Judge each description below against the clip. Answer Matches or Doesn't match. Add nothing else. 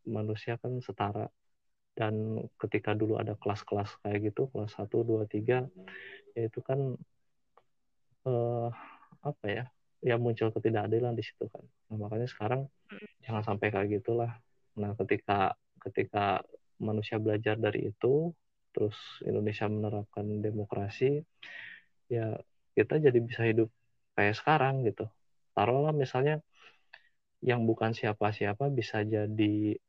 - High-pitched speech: Doesn't match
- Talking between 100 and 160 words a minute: Matches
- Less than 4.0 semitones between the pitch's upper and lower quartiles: Matches